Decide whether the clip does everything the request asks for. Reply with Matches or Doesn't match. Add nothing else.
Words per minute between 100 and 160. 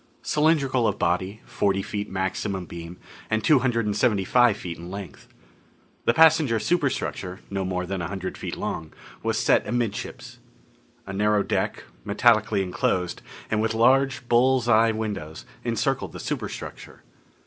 Matches